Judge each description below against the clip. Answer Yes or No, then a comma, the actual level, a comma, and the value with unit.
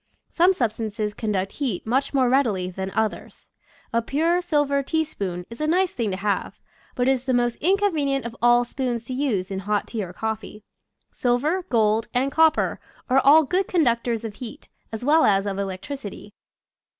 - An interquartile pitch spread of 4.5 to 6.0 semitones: Yes, average, 5.2 semitones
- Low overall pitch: No, high, 240 Hz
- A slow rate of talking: No, average, 180 wpm